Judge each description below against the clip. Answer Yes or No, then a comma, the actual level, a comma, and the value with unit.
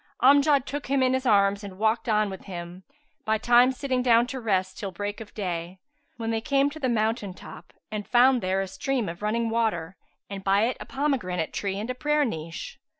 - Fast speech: Yes, fast, 210 wpm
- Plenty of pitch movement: No, average, 4.7 semitones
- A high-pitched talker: Yes, high, 220 Hz